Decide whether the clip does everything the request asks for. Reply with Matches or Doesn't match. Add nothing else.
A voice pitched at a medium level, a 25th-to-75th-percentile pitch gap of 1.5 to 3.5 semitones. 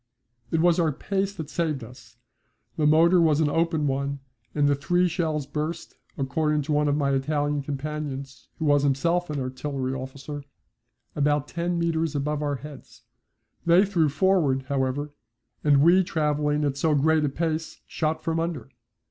Matches